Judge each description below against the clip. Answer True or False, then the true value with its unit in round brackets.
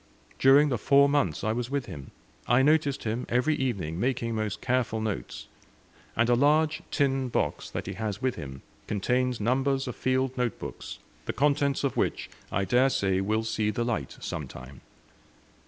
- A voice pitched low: True (125 Hz)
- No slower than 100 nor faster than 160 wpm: False (175 wpm)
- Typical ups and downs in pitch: True (3.8 semitones)